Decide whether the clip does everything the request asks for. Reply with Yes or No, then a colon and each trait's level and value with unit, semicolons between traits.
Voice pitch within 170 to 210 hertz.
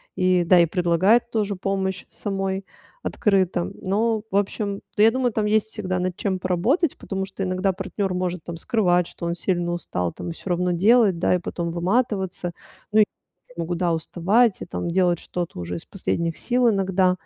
Yes: medium, 185 Hz